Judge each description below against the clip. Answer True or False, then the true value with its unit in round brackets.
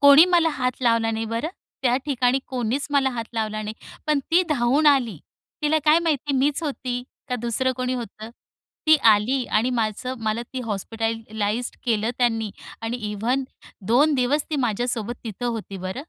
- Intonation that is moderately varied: True (3.5 semitones)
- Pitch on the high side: True (245 Hz)